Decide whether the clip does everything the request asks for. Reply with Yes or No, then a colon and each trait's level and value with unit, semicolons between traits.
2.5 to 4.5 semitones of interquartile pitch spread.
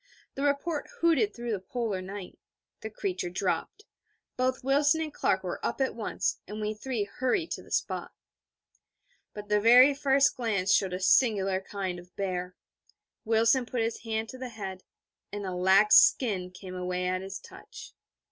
No: average, 5.2 semitones